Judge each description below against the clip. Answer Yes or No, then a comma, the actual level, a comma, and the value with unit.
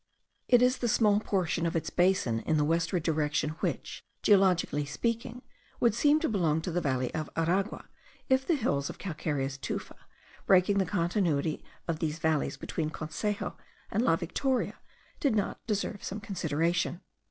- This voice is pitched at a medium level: Yes, medium, 175 Hz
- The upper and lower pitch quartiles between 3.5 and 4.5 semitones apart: No, average, 5.1 semitones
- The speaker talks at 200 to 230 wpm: No, average, 160 wpm